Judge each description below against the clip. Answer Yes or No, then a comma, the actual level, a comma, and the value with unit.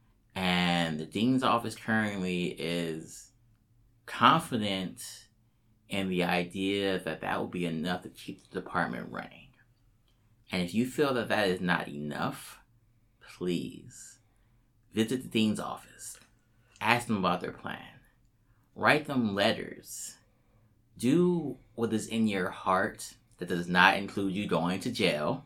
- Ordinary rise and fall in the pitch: Yes, average, 4.2 semitones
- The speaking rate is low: Yes, slow, 130 wpm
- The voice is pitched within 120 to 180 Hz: No, low, 110 Hz